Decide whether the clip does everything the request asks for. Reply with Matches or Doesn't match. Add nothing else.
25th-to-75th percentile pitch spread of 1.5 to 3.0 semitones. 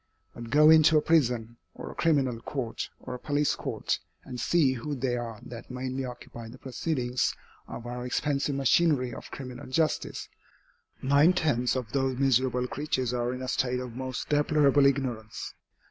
Matches